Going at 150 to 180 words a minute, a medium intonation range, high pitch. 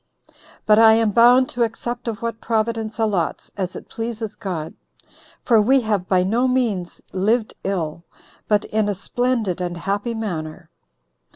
Yes: average, 155 wpm; average, 3.5 semitones; high, 215 Hz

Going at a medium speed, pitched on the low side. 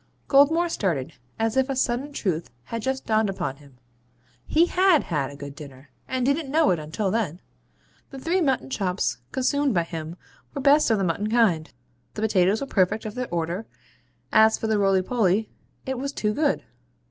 No: average, 180 wpm; high, 220 Hz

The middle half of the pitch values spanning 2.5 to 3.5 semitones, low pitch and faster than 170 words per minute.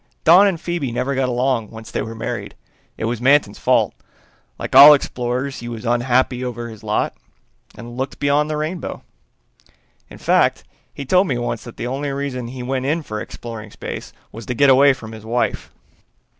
Yes: average, 3.1 semitones; low, 125 Hz; average, 185 wpm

